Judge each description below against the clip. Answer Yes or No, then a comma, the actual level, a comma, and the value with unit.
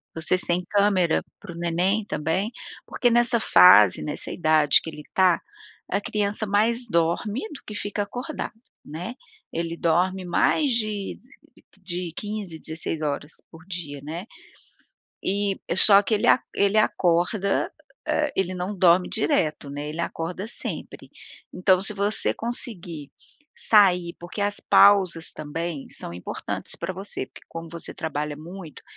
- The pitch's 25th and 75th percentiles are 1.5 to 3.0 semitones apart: No, average, 3.9 semitones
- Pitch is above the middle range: No, medium, 180 Hz